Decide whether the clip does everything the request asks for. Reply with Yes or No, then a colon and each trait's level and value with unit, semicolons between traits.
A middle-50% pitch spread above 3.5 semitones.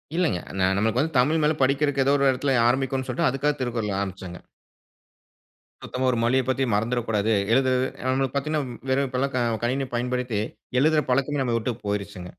No: average, 2.8 semitones